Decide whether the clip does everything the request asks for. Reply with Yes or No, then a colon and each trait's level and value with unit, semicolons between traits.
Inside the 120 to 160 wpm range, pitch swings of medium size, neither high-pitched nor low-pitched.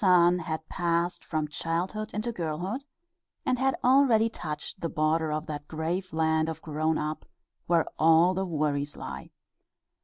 Yes: average, 150 wpm; average, 3.1 semitones; medium, 165 Hz